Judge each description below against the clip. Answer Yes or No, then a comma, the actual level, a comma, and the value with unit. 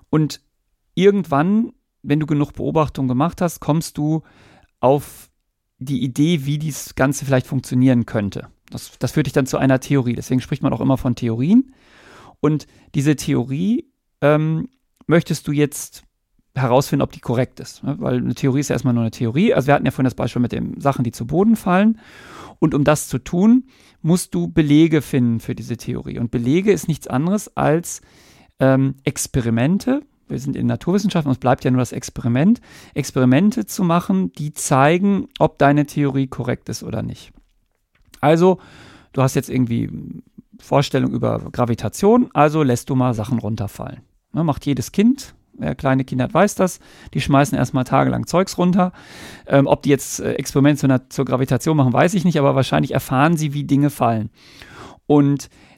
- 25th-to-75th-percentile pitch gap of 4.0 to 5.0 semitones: Yes, average, 4.3 semitones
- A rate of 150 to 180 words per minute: Yes, average, 170 wpm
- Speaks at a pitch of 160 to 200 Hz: No, medium, 140 Hz